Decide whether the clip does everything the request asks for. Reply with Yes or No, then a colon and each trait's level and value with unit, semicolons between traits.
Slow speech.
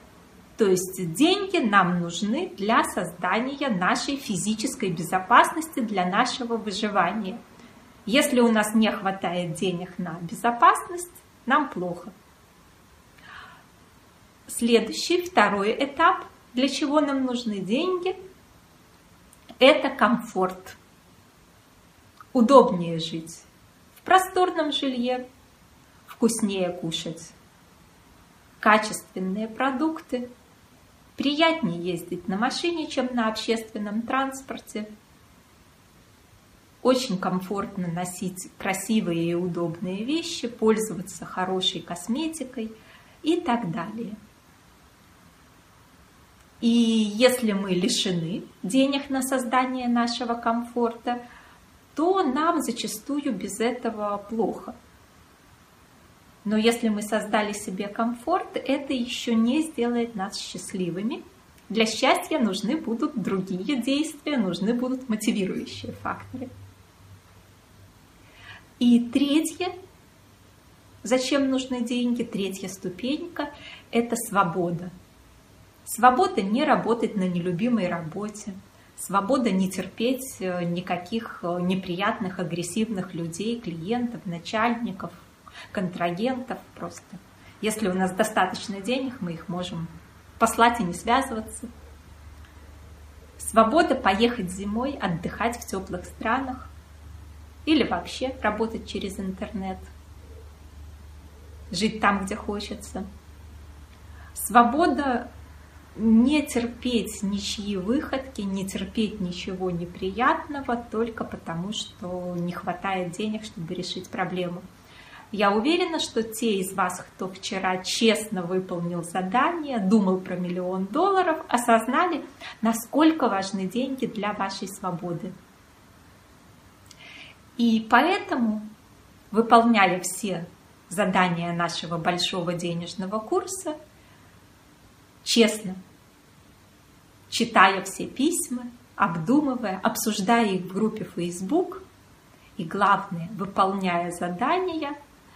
Yes: slow, 90 wpm